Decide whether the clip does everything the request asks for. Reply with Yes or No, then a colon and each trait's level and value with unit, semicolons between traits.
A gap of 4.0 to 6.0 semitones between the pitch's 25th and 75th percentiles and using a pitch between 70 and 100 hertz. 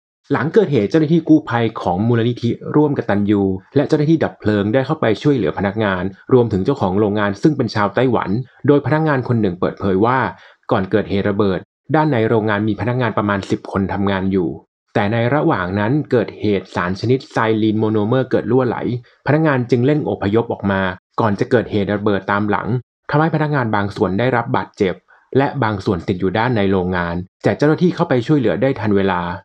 No: average, 5.0 semitones; low, 110 Hz